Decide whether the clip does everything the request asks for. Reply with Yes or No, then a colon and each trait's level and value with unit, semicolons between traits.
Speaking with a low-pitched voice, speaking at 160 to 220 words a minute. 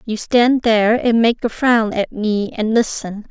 No: high, 225 Hz; average, 200 wpm